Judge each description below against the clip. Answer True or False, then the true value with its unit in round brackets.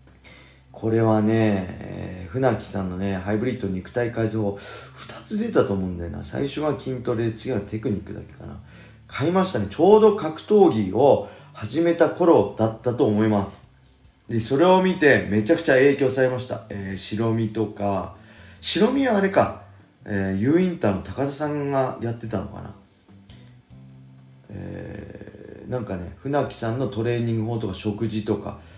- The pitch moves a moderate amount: True (4.4 semitones)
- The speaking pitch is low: True (110 Hz)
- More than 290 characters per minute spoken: True (315 characters per minute)